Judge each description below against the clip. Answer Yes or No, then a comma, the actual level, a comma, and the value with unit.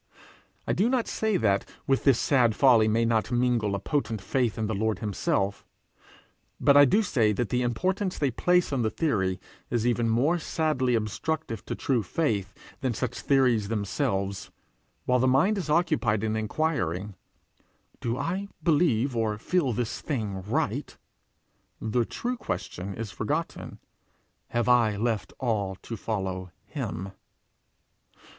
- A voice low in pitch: Yes, low, 120 Hz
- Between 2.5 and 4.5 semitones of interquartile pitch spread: No, average, 5.1 semitones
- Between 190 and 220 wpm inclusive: No, average, 145 wpm